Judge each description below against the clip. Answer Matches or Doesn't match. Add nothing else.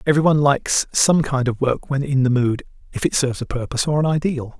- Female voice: Doesn't match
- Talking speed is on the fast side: Matches